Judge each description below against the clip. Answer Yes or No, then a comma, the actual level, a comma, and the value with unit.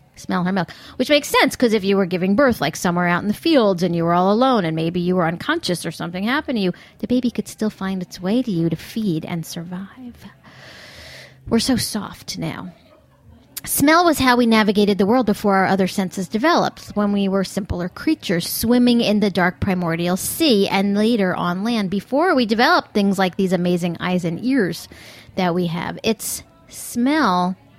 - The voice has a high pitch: Yes, high, 200 Hz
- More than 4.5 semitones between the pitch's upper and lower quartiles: Yes, average, 4.9 semitones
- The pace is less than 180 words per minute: No, average, 200 wpm